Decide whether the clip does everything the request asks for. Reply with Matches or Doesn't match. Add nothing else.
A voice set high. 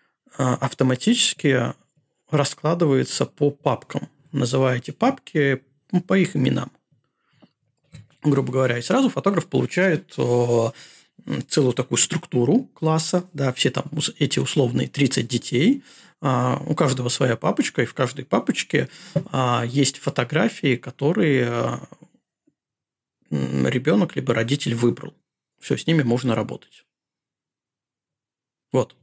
Doesn't match